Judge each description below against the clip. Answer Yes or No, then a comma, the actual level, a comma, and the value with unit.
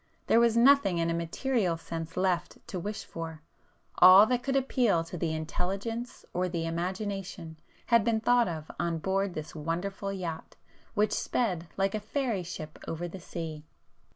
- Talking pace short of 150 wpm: No, average, 160 wpm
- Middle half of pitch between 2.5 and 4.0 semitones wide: No, average, 4.6 semitones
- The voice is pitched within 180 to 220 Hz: Yes, medium, 185 Hz